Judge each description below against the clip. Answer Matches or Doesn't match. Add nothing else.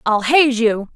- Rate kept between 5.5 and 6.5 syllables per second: Doesn't match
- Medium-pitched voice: Doesn't match